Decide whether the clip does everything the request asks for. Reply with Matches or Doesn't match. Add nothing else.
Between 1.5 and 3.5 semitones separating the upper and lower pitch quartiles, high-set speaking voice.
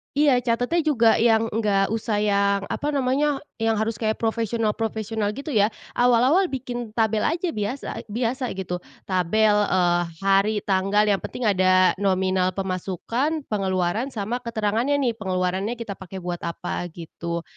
Doesn't match